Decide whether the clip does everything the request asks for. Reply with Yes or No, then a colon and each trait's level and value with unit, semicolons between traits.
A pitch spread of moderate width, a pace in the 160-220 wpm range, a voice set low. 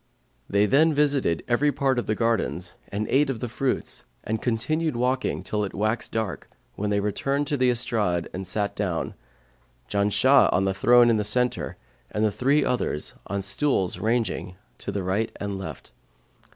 Yes: average, 4.3 semitones; average, 180 wpm; low, 110 Hz